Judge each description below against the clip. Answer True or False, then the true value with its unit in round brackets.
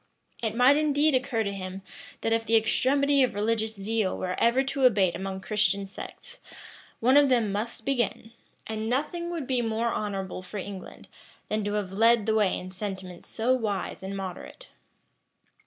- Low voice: False (220 Hz)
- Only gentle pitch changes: False (4.2 semitones)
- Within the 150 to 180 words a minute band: True (175 wpm)